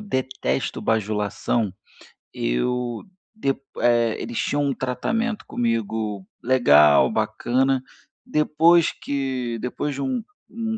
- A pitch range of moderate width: Yes, average, 4.1 semitones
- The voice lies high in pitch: No, low, 125 Hz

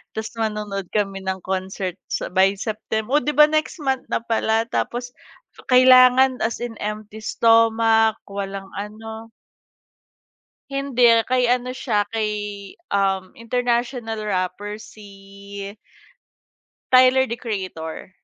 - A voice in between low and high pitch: No, high, 220 Hz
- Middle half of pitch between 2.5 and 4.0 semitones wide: Yes, average, 3.5 semitones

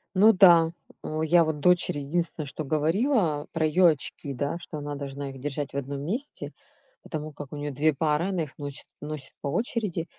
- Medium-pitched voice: Yes, medium, 155 Hz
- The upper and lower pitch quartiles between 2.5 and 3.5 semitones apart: Yes, average, 3.1 semitones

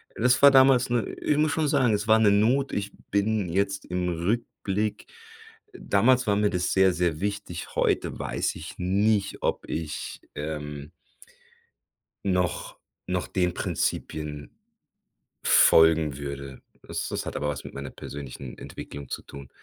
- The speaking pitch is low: Yes, very low, 95 Hz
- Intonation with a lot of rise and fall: Yes, wide, 6.1 semitones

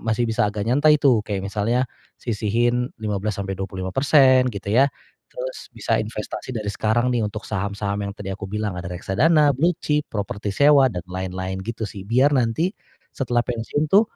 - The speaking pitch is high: No, low, 110 Hz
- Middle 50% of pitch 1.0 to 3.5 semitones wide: No, average, 4.5 semitones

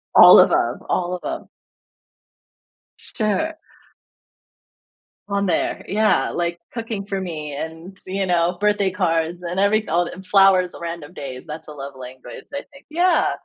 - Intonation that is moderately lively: Yes, average, 3.6 semitones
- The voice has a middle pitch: Yes, medium, 180 Hz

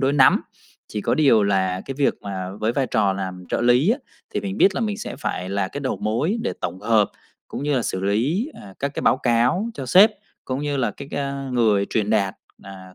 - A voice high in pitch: No, low, 120 Hz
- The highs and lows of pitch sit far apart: Yes, wide, 6.2 semitones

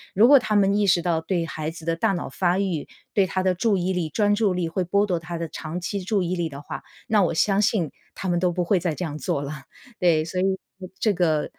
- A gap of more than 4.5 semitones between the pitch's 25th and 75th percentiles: No, average, 3.0 semitones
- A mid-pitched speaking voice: Yes, medium, 180 Hz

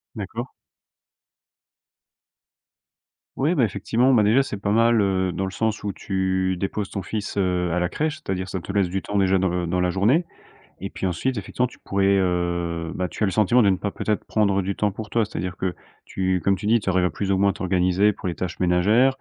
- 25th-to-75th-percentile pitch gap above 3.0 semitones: No, average, 2.7 semitones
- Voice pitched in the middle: No, very low, 95 Hz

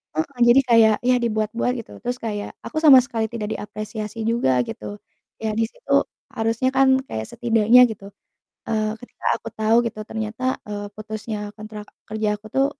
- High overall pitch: Yes, high, 220 Hz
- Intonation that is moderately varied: No, narrow, 1.8 semitones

